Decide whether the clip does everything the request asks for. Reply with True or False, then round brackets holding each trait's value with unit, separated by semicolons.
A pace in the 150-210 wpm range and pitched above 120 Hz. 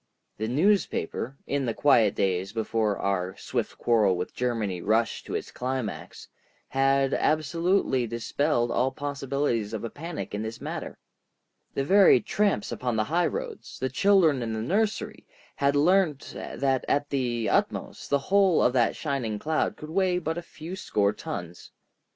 True (155 wpm; 135 Hz)